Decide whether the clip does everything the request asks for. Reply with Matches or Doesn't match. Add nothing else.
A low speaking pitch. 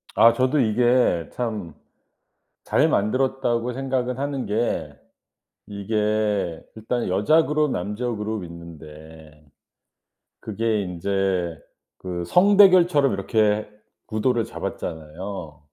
Matches